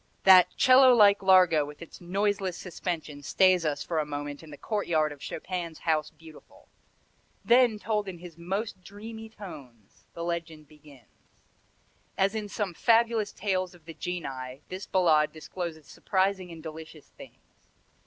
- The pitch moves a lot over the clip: No, average, 4.4 semitones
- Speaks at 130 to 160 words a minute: Yes, average, 150 wpm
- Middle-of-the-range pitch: Yes, medium, 175 Hz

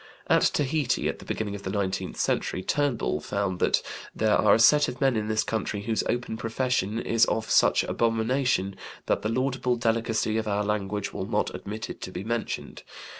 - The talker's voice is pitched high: No, low, 110 Hz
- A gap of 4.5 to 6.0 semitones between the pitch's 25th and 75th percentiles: No, average, 2.9 semitones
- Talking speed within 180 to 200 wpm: Yes, average, 190 wpm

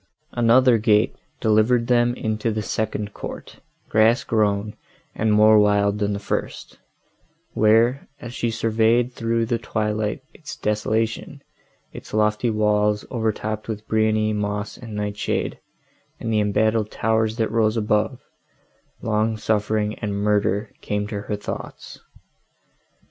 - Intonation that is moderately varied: No, narrow, 1.3 semitones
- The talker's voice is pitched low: Yes, low, 110 Hz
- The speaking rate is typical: No, slow, 120 wpm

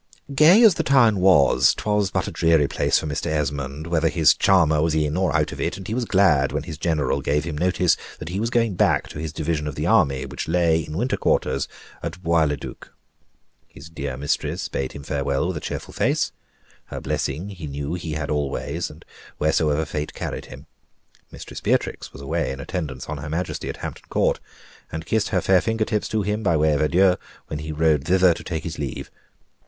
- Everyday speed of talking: No, fast, 210 wpm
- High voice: No, very low, 80 Hz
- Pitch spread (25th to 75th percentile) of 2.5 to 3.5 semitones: No, average, 3.9 semitones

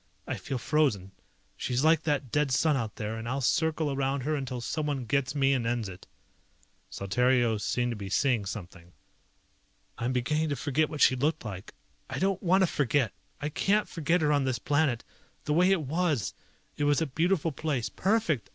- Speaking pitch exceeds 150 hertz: No, medium, 140 Hz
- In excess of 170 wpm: Yes, average, 190 wpm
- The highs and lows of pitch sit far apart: No, average, 4.5 semitones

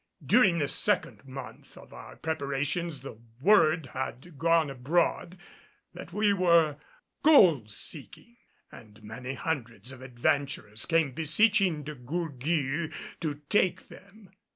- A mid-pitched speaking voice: Yes, medium, 155 Hz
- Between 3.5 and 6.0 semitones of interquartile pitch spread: Yes, average, 4.6 semitones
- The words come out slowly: Yes, slow, 120 wpm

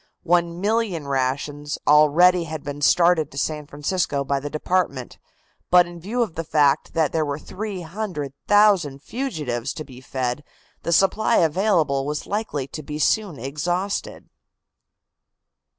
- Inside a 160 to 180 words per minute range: No, slow, 135 wpm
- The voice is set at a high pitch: No, medium, 155 Hz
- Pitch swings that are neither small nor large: Yes, average, 4.1 semitones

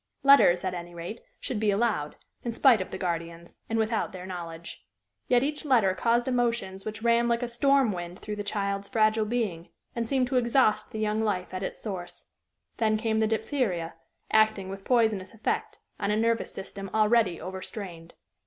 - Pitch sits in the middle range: No, high, 215 Hz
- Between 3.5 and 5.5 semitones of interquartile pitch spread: Yes, average, 3.8 semitones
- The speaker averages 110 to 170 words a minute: No, average, 180 wpm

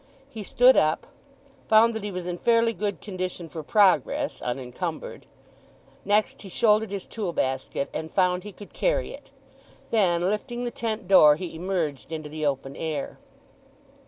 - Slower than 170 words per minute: Yes, average, 160 wpm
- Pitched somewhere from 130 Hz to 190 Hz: Yes, medium, 185 Hz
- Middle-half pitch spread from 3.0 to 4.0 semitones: No, average, 5.3 semitones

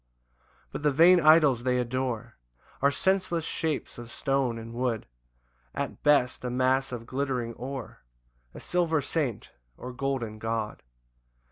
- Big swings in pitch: No, average, 3.6 semitones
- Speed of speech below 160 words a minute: Yes, average, 140 wpm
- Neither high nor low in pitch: No, low, 130 Hz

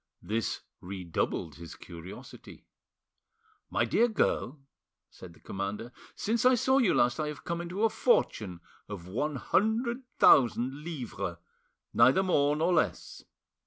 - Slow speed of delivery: Yes, slow, 130 wpm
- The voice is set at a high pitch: No, low, 135 Hz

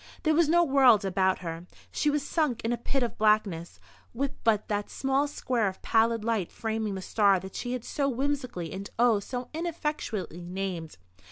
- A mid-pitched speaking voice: No, high, 225 Hz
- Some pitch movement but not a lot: No, wide, 5.9 semitones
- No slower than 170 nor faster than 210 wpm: Yes, average, 185 wpm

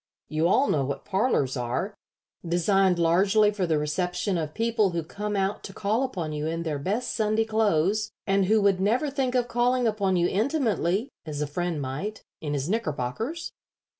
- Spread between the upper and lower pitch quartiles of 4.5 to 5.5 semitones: Yes, average, 5.2 semitones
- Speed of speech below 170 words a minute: No, average, 180 wpm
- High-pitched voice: Yes, high, 195 Hz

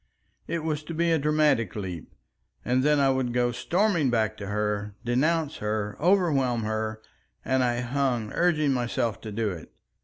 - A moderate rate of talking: Yes, average, 165 wpm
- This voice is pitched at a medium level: No, low, 125 Hz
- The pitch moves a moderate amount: No, wide, 5.7 semitones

